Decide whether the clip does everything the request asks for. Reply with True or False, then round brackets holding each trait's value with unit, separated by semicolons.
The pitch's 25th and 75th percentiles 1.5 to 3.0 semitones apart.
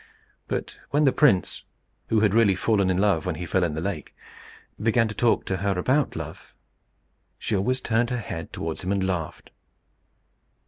False (4.1 semitones)